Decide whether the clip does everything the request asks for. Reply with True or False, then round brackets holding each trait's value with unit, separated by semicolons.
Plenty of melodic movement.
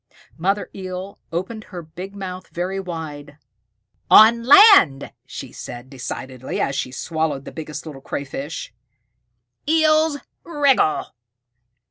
True (6.9 semitones)